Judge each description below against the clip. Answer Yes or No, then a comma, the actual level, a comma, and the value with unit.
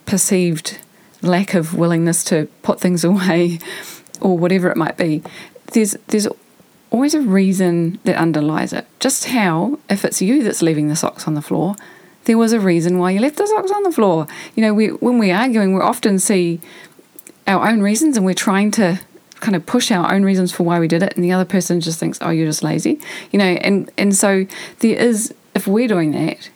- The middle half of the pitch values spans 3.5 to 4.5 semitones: Yes, average, 4.2 semitones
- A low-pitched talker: No, high, 195 Hz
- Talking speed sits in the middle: No, fast, 210 wpm